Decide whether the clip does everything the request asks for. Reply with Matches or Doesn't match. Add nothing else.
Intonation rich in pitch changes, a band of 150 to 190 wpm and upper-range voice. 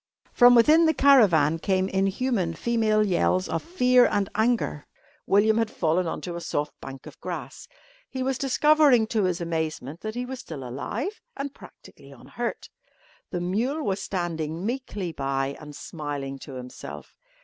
Matches